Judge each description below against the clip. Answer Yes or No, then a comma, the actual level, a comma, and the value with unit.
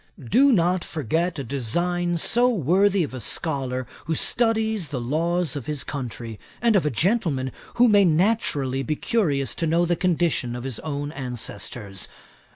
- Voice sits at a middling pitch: Yes, medium, 160 Hz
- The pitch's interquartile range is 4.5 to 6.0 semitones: Yes, wide, 5.6 semitones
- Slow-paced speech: No, average, 160 wpm